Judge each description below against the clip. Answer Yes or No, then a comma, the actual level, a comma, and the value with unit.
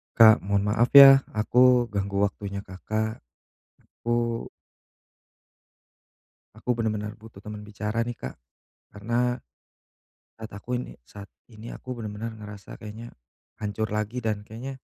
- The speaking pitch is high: No, low, 110 Hz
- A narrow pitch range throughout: Yes, narrow, 2.3 semitones